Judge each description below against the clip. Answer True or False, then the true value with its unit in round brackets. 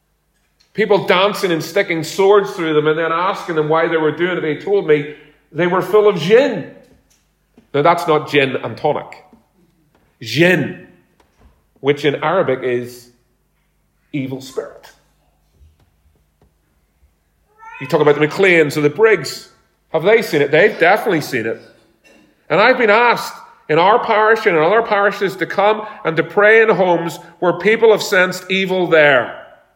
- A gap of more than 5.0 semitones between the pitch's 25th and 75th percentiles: True (5.4 semitones)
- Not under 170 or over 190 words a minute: False (155 wpm)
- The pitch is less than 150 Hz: False (165 Hz)